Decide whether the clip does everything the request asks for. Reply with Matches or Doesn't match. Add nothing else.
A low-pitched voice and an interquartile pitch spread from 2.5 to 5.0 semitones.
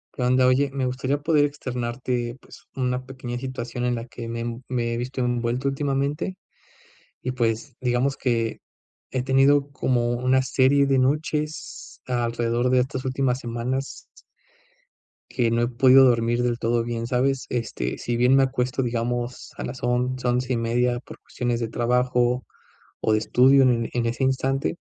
Doesn't match